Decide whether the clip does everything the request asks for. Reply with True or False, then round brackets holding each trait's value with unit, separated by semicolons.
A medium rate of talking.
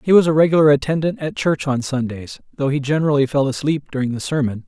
False (220 wpm)